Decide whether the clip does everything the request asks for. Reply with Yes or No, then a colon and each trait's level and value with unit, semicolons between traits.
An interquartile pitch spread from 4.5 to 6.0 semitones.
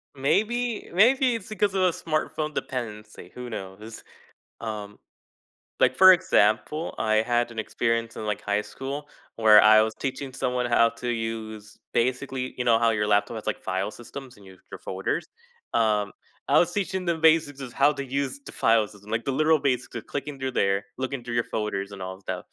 Yes: average, 4.9 semitones